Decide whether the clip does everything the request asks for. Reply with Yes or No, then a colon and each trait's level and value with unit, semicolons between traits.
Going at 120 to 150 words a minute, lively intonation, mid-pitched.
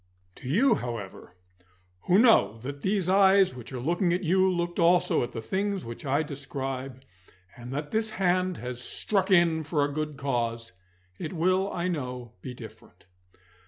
No: average, 165 wpm; wide, 6.6 semitones; medium, 155 Hz